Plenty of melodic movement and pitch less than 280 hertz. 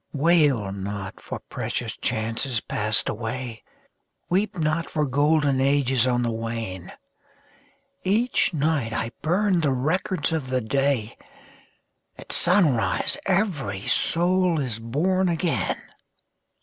Yes: wide, 6.8 semitones; medium, 140 Hz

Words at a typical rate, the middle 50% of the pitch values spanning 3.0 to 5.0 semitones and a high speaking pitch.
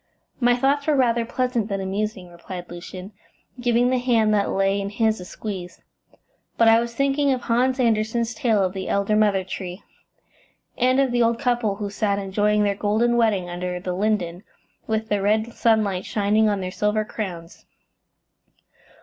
Yes: average, 170 wpm; average, 3.4 semitones; high, 215 Hz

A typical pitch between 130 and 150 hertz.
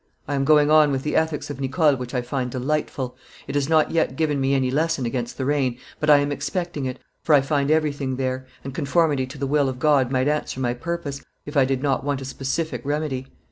Yes: medium, 140 Hz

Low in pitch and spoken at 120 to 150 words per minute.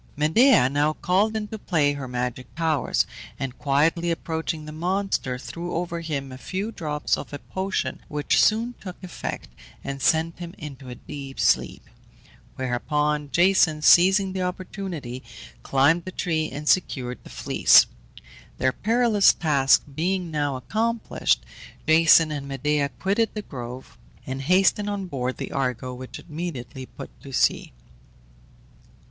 No: medium, 155 Hz; average, 140 wpm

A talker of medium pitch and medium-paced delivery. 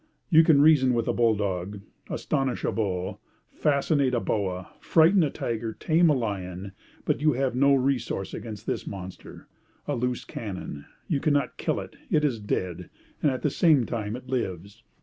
No: low, 120 Hz; average, 175 wpm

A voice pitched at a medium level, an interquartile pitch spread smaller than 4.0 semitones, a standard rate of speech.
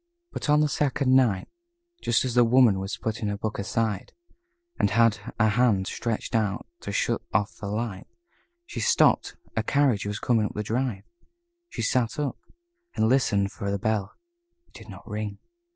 No: low, 110 Hz; average, 3.4 semitones; average, 175 wpm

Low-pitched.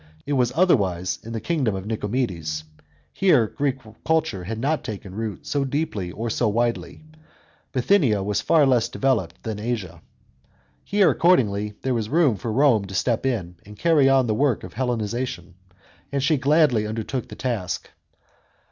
Yes: low, 115 Hz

